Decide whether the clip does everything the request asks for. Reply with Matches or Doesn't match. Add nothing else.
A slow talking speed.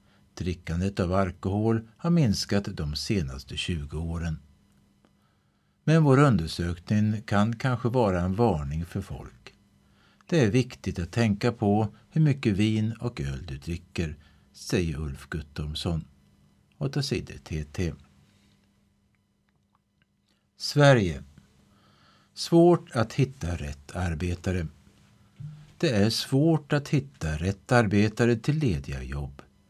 Matches